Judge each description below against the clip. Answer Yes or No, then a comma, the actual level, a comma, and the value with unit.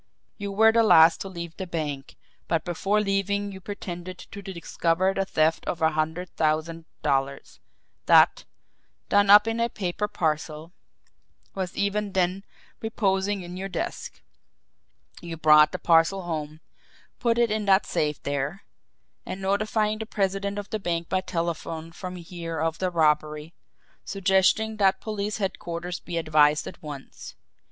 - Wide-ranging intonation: No, average, 3.6 semitones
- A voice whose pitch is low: No, medium, 180 Hz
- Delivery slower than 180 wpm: Yes, average, 150 wpm